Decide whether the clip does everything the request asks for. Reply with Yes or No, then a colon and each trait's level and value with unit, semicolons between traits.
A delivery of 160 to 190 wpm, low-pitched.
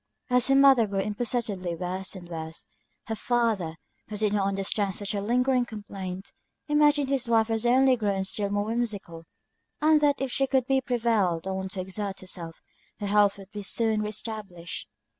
No: average, 180 wpm; high, 210 Hz